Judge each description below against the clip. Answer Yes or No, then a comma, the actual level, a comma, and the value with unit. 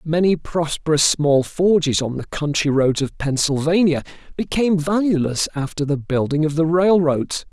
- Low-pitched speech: No, medium, 155 Hz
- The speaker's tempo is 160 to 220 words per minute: No, average, 145 wpm